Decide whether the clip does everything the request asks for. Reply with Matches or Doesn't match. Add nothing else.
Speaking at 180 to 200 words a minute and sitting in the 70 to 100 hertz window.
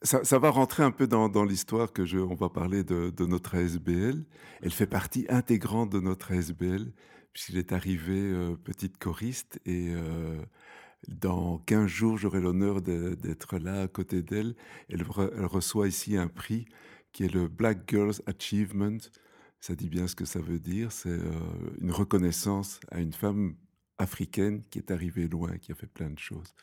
Matches